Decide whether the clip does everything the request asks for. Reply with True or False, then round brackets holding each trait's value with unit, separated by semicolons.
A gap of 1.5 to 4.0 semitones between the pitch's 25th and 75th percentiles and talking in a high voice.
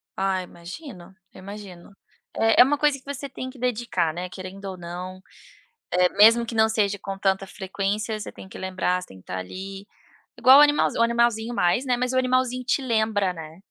False (4.7 semitones; 205 Hz)